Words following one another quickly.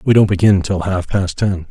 Yes: fast, 245 wpm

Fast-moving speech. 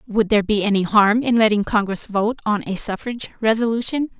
No: average, 185 wpm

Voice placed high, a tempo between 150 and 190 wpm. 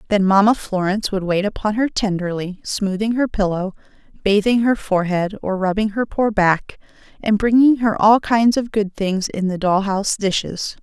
Yes: high, 205 Hz; average, 175 wpm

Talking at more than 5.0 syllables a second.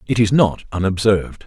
Yes: 5.5 syllables/s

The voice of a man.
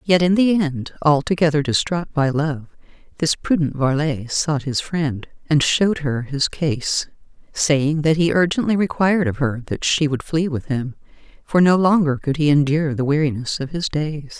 No: female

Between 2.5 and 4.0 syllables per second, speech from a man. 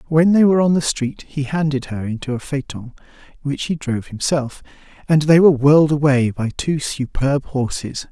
No: 5.2 syllables/s; male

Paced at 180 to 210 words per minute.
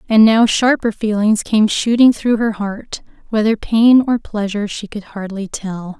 No: average, 170 wpm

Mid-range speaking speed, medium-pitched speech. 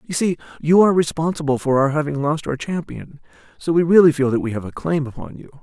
No: fast, 235 wpm; medium, 150 Hz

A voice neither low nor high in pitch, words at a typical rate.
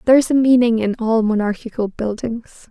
No: high, 230 Hz; average, 175 wpm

